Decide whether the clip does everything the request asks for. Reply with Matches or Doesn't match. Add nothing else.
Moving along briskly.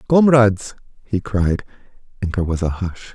Doesn't match